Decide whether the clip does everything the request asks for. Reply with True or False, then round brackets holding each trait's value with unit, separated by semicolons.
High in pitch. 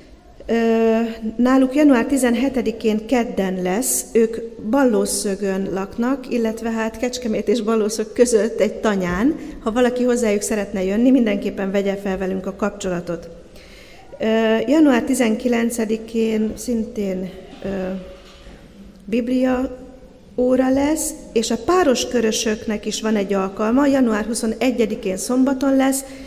True (225 Hz)